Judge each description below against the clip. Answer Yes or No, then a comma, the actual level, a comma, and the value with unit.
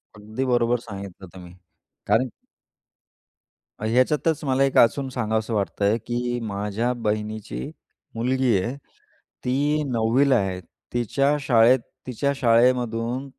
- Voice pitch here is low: Yes, low, 120 Hz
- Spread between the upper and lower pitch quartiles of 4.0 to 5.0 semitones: No, average, 3.3 semitones